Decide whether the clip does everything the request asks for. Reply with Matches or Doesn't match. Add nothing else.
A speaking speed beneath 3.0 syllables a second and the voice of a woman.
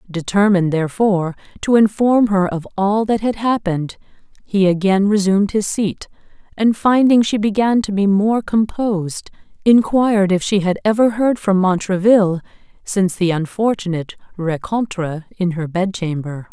Doesn't match